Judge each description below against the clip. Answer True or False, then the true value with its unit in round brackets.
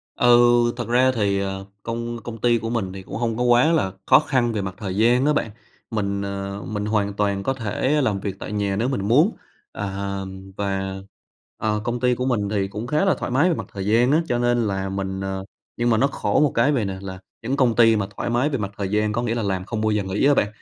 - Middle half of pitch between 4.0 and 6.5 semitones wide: False (3.6 semitones)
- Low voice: True (110 Hz)